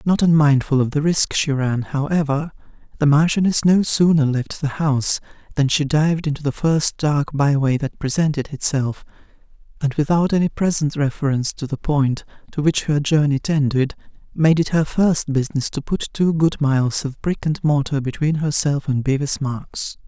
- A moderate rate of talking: Yes, average, 175 wpm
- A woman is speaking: No, male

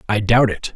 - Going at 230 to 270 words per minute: Yes, fast, 235 wpm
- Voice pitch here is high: No, low, 110 Hz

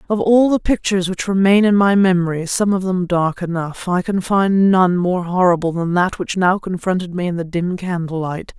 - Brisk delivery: Yes, fast, 215 wpm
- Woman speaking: Yes, female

